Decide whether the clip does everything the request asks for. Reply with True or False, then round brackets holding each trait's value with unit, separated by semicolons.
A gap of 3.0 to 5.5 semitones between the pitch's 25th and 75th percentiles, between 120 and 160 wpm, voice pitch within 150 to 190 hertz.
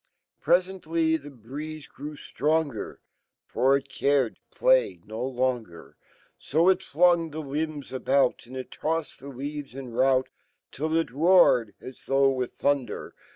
False (3.6 semitones; 135 wpm; 140 Hz)